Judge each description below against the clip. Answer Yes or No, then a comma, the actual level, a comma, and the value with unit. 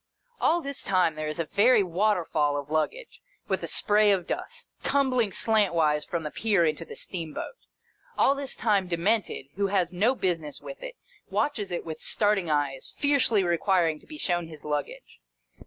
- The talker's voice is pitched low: No, medium, 185 Hz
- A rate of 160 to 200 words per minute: Yes, average, 175 wpm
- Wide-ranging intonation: Yes, wide, 5.7 semitones